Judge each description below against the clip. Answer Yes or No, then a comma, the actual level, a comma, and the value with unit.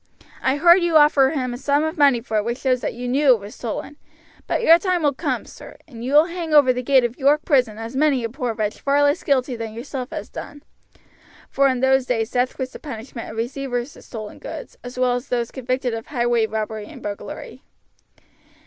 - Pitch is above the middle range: Yes, very high, 255 Hz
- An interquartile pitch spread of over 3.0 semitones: Yes, average, 3.4 semitones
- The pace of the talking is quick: Yes, fast, 230 wpm